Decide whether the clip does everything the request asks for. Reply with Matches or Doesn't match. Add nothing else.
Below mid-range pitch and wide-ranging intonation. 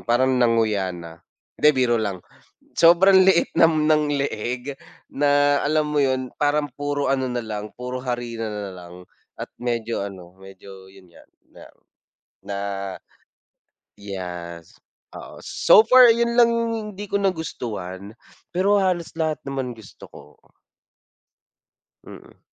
Matches